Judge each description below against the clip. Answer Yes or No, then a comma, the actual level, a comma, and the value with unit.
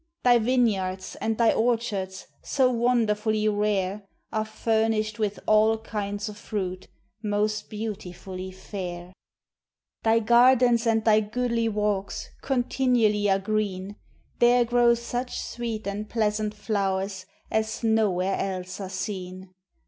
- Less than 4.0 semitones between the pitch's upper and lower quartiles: Yes, average, 2.7 semitones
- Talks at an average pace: No, slow, 120 wpm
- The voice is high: Yes, high, 215 Hz